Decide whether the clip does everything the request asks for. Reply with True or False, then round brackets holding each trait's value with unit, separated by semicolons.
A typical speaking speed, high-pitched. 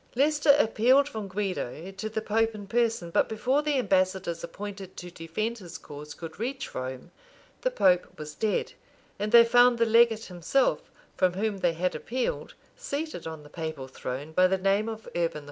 True (180 wpm; 205 Hz)